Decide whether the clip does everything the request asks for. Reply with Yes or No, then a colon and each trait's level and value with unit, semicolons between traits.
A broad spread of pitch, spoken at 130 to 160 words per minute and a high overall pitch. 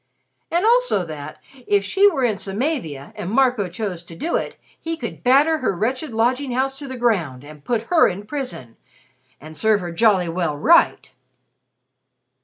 No: wide, 7.7 semitones; average, 175 wpm; high, 220 Hz